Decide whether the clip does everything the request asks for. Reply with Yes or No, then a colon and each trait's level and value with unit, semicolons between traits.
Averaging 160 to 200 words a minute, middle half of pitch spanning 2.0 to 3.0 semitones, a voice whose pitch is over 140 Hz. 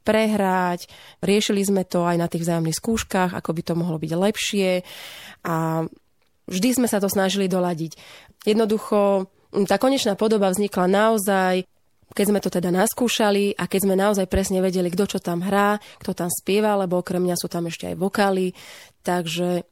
Yes: fast, 165 wpm; narrow, 2.5 semitones; high, 190 Hz